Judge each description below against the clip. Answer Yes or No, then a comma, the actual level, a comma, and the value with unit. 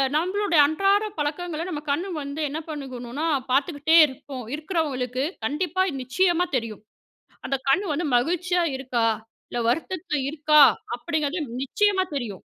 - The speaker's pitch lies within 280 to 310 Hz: Yes, very high, 300 Hz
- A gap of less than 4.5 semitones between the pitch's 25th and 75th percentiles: No, average, 4.8 semitones